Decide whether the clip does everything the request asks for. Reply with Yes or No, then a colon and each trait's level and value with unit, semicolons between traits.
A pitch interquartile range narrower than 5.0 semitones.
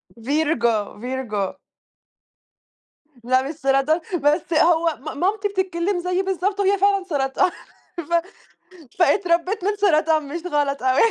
No: wide, 5.5 semitones